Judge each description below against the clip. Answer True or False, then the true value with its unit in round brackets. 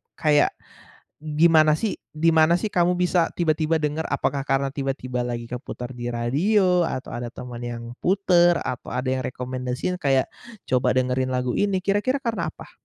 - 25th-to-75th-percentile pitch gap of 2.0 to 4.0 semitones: False (5.5 semitones)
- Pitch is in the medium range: True (150 Hz)